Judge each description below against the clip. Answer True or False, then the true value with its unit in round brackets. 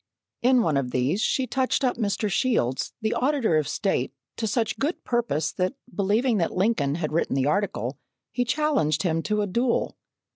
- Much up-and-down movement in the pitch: True (7.9 semitones)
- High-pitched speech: True (205 Hz)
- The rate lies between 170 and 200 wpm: True (180 wpm)